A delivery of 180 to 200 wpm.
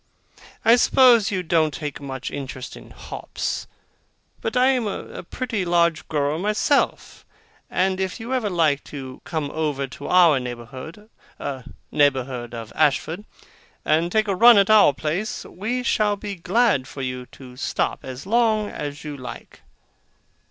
No: average, 150 wpm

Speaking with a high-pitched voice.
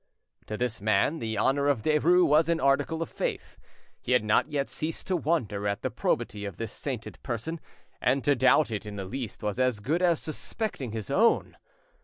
No: low, 130 Hz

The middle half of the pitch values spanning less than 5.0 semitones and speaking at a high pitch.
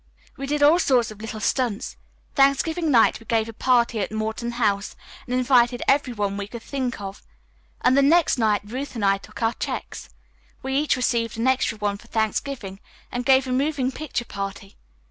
Yes: average, 3.7 semitones; high, 240 Hz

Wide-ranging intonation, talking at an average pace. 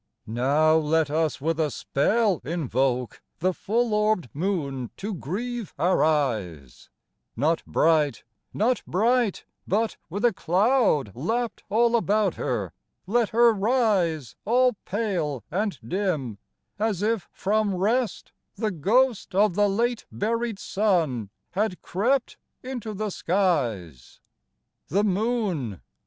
No: wide, 6.4 semitones; slow, 120 wpm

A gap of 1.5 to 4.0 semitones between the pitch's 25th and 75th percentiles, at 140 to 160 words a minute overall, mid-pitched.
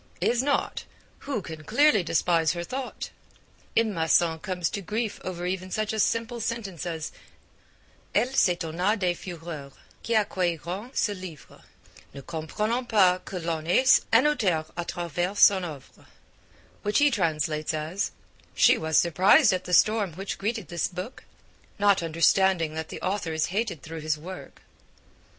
No: average, 4.4 semitones; average, 150 wpm; medium, 180 Hz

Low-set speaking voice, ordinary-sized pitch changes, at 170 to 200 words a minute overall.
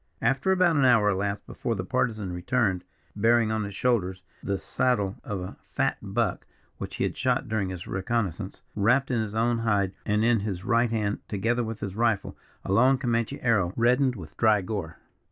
Yes: low, 110 Hz; average, 3.3 semitones; average, 185 wpm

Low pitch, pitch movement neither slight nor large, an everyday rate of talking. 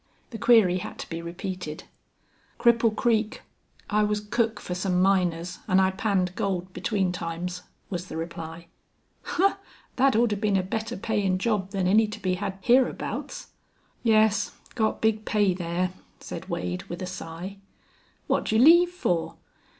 No: high, 195 Hz; average, 3.4 semitones; average, 155 wpm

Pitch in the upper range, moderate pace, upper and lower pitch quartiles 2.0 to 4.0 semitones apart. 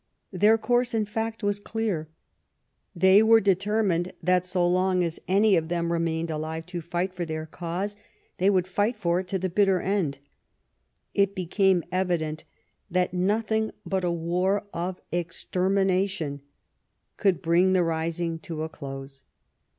No: medium, 180 Hz; average, 150 wpm; average, 2.9 semitones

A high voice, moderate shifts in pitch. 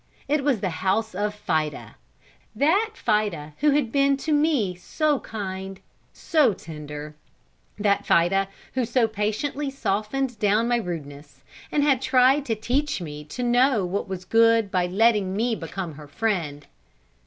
No: high, 215 Hz; wide, 6.1 semitones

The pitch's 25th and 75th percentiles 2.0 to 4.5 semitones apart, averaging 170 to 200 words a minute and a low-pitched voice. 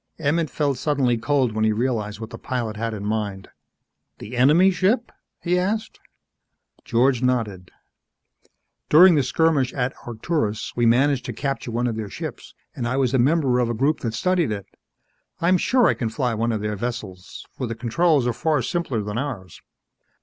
No: average, 4.9 semitones; average, 180 wpm; low, 125 Hz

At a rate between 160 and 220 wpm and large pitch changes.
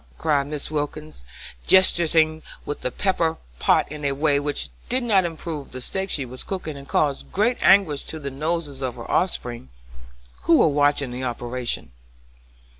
No: average, 165 wpm; average, 3.3 semitones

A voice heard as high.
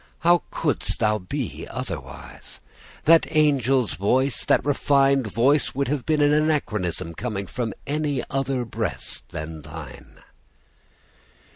No: low, 130 Hz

